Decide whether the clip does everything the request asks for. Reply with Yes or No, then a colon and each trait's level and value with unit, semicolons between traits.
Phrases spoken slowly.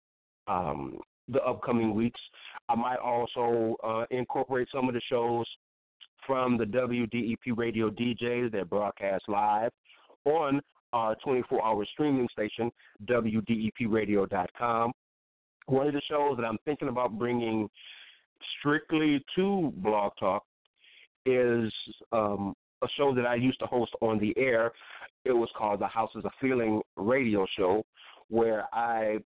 Yes: slow, 130 wpm